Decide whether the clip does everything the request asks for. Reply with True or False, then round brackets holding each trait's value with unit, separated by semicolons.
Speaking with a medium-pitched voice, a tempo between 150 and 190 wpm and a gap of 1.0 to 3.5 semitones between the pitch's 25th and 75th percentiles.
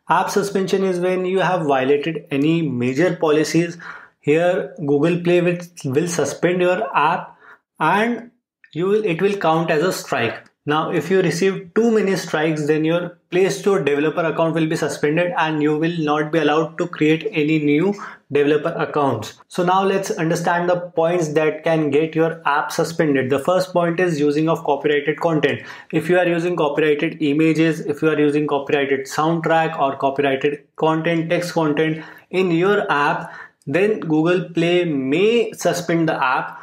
True (165 Hz; 165 wpm; 2.8 semitones)